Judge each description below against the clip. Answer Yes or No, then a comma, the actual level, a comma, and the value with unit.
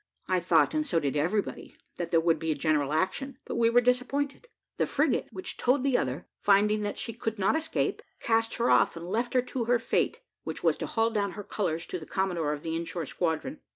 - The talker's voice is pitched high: Yes, high, 200 Hz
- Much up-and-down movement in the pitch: Yes, wide, 6.7 semitones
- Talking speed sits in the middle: No, fast, 230 wpm